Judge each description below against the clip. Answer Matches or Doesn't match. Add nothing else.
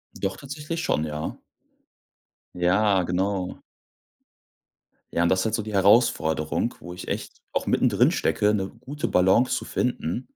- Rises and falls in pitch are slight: Doesn't match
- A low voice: Matches